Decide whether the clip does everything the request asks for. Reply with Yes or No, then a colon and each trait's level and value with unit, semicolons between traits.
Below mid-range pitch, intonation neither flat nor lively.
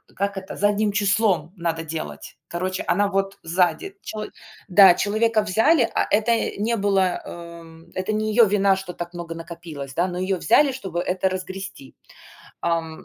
No: high, 190 Hz; average, 3.2 semitones